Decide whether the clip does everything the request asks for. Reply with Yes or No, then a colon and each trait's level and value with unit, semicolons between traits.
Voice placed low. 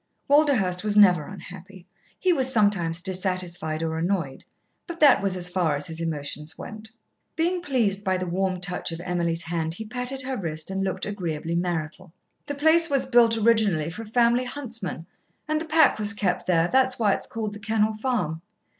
No: high, 195 Hz